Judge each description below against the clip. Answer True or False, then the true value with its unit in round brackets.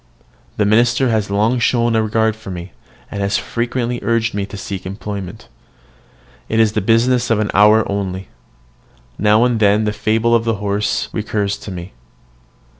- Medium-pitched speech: False (110 Hz)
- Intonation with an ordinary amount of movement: False (2.3 semitones)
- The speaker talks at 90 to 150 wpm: False (170 wpm)